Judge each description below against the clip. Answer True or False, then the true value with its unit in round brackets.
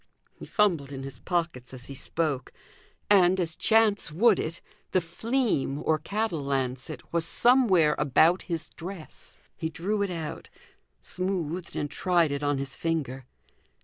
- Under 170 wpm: True (145 wpm)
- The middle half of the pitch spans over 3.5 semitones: True (4.9 semitones)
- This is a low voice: False (165 Hz)